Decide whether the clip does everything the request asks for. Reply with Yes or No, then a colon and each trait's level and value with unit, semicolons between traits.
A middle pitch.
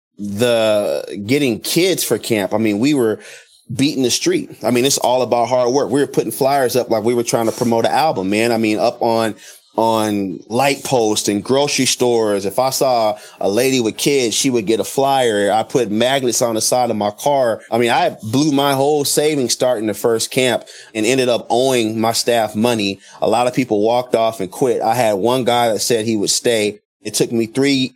No: low, 115 Hz